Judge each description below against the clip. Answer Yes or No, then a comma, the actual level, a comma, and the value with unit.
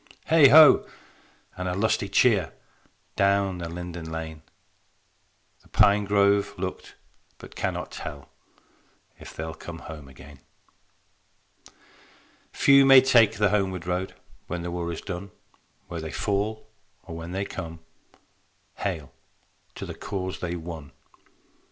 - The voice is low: Yes, very low, 90 Hz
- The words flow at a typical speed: No, slow, 125 wpm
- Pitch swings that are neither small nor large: Yes, average, 3.6 semitones